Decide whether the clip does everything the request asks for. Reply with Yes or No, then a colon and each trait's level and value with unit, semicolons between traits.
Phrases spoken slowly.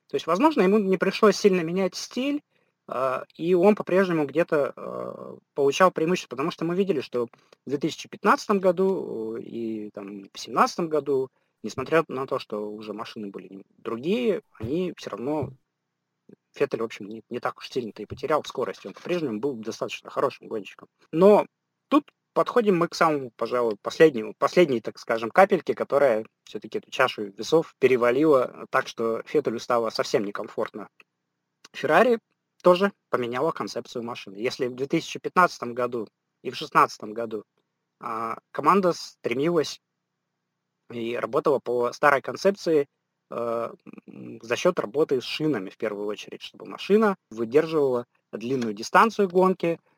No: average, 140 wpm